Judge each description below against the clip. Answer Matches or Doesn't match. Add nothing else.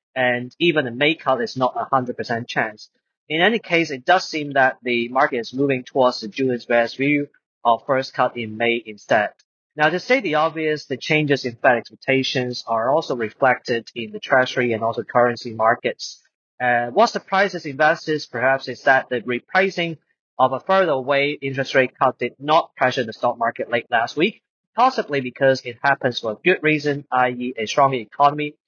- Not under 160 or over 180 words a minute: Doesn't match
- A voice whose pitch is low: Matches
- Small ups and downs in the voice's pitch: Doesn't match